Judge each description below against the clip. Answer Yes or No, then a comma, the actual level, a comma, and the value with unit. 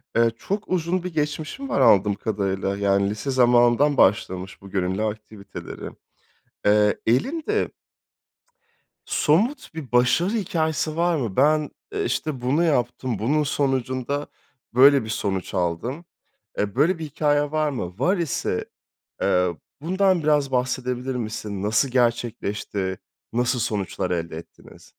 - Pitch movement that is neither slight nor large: No, wide, 6.8 semitones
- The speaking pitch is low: Yes, low, 125 Hz